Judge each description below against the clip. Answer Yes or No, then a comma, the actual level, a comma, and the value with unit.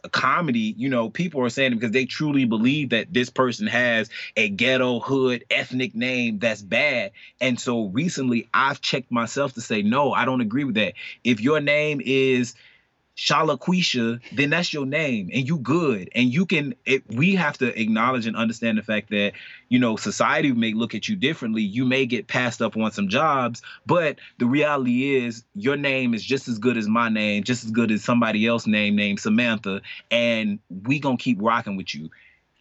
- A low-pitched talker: Yes, low, 125 Hz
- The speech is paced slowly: No, average, 195 wpm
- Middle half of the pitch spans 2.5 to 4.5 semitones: Yes, average, 3.2 semitones